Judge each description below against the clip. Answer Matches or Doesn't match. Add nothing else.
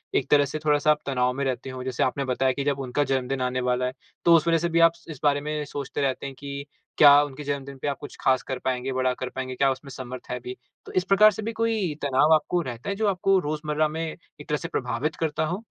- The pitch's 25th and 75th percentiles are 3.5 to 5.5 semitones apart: Doesn't match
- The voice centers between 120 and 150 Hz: Matches